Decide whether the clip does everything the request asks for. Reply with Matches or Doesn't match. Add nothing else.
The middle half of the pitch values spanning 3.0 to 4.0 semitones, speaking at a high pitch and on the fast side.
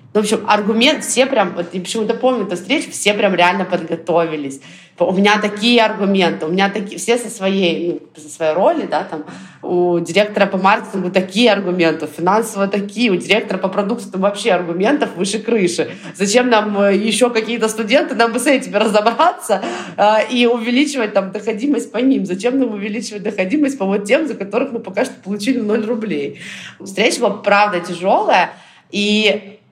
Matches